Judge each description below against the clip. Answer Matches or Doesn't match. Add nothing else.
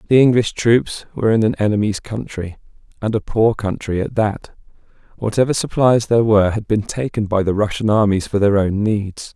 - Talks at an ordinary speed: Matches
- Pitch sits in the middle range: Doesn't match